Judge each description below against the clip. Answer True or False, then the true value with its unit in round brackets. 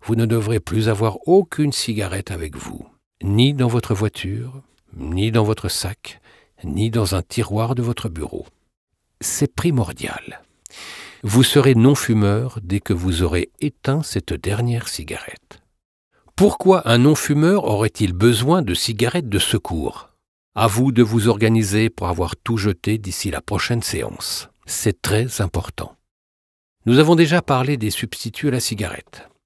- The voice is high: False (110 Hz)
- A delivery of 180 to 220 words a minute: False (145 wpm)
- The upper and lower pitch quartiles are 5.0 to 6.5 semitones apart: False (3.9 semitones)